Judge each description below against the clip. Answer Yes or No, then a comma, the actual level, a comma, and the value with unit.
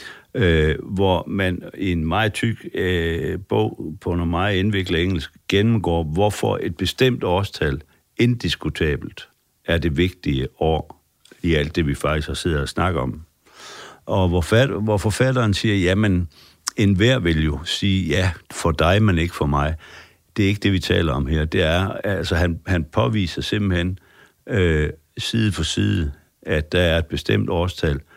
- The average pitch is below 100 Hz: Yes, very low, 90 Hz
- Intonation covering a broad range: No, average, 3.6 semitones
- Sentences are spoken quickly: No, average, 160 wpm